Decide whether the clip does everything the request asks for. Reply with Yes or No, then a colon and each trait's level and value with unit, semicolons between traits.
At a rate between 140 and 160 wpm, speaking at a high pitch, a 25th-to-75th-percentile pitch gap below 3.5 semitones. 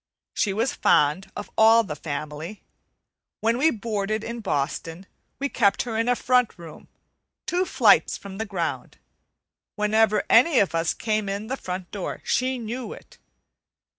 No: average, 155 wpm; high, 215 Hz; average, 3.9 semitones